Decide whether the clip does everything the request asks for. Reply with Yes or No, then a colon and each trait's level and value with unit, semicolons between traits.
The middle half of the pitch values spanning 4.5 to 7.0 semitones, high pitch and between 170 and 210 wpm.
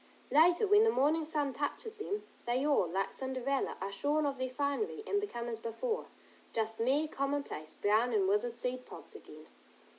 Yes: average, 5.1 semitones; very high, 275 Hz; average, 175 wpm